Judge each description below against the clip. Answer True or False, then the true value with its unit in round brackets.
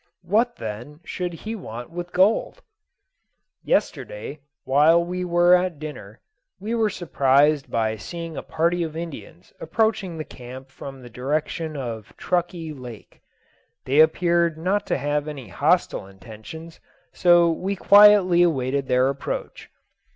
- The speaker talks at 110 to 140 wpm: True (135 wpm)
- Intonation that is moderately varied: True (5.0 semitones)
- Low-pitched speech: False (160 Hz)